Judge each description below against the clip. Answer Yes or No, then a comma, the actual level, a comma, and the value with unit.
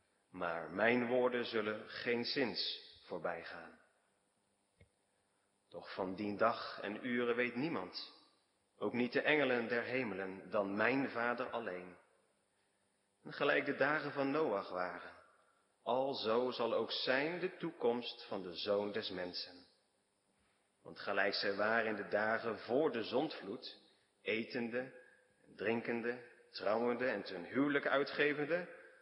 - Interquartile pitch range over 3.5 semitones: Yes, average, 4.0 semitones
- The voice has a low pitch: Yes, low, 115 Hz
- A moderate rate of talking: No, slow, 130 wpm